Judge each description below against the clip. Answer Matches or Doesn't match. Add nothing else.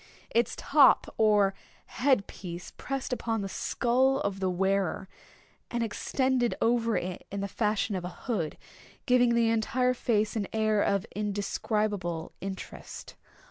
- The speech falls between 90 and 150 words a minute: Matches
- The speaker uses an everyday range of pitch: Matches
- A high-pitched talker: Matches